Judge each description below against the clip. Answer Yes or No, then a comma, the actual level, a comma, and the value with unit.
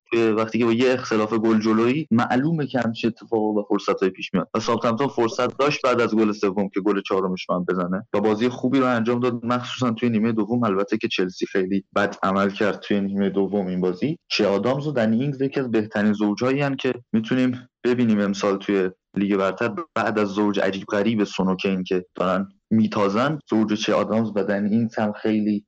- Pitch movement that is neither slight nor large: Yes, average, 3.4 semitones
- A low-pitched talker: Yes, low, 110 Hz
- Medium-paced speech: No, fast, 200 wpm